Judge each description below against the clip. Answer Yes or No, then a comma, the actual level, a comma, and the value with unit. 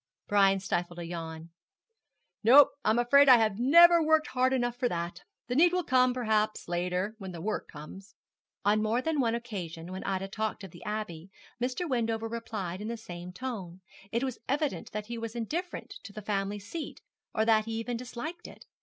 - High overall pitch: Yes, high, 220 Hz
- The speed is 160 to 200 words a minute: Yes, average, 190 wpm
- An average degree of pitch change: Yes, average, 4.6 semitones